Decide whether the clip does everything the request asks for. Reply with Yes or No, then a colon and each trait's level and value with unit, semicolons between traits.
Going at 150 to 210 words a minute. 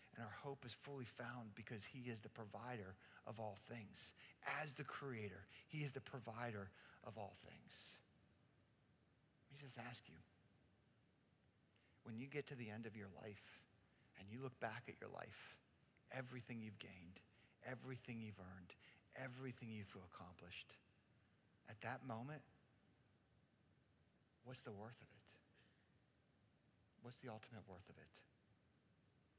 No: average, 140 wpm